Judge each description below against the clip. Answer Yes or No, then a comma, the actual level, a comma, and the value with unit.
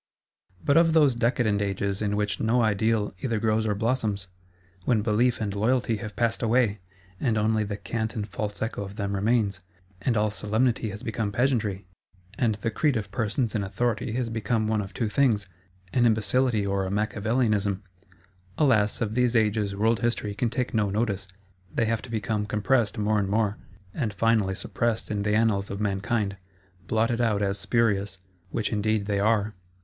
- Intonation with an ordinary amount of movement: No, narrow, 2.3 semitones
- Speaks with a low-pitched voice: Yes, low, 110 Hz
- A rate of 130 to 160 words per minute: No, average, 175 wpm